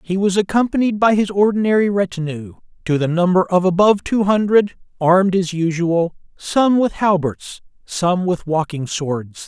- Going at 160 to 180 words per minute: No, average, 150 wpm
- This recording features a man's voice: Yes, male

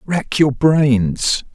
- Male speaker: Yes, male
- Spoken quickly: No, slow, 115 wpm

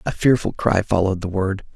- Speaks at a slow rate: No, fast, 205 wpm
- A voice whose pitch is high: No, low, 100 Hz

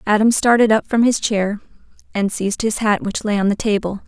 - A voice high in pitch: Yes, high, 210 Hz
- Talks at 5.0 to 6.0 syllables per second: Yes, 5.6 syllables/s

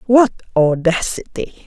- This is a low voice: No, high, 195 Hz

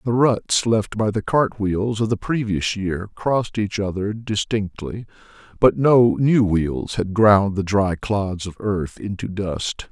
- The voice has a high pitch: No, low, 105 Hz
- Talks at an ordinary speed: Yes, average, 170 wpm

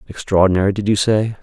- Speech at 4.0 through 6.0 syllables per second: No, 6.5 syllables/s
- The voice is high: No, low, 100 Hz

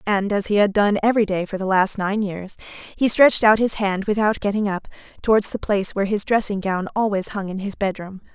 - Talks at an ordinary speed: No, fast, 230 wpm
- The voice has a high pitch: Yes, high, 200 Hz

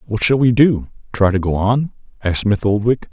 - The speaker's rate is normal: Yes, average, 190 wpm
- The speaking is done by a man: Yes, male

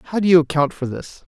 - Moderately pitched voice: Yes, medium, 160 Hz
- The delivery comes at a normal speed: No, fast, 270 wpm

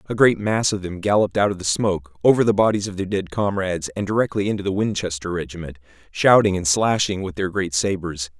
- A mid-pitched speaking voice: No, very low, 95 Hz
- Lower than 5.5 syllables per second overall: No, 6.0 syllables/s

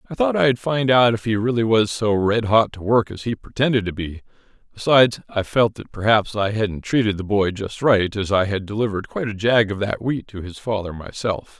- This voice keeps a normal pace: No, fast, 235 wpm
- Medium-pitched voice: No, low, 110 Hz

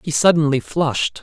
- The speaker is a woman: No, male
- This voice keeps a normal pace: Yes, average, 145 wpm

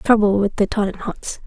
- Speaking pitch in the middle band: No, high, 205 Hz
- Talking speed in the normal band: Yes, average, 165 wpm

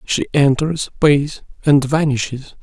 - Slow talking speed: Yes, slow, 115 wpm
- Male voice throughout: Yes, male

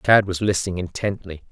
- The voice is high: No, very low, 95 Hz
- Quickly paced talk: No, average, 160 wpm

